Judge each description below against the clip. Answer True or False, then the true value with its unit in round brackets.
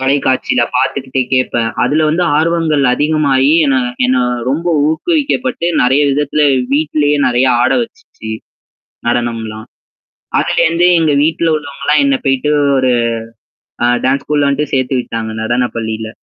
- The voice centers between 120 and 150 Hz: True (140 Hz)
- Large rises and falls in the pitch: False (3.5 semitones)